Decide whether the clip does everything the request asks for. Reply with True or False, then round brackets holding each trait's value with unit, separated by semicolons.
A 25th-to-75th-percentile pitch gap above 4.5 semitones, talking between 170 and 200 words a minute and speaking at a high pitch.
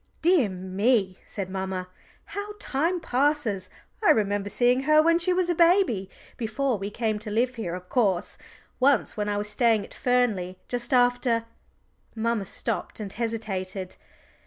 False (5.1 semitones; 160 wpm; 230 Hz)